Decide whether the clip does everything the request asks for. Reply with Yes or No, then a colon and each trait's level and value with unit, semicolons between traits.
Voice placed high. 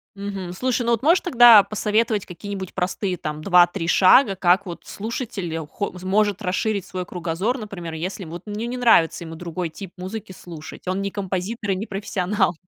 Yes: high, 195 Hz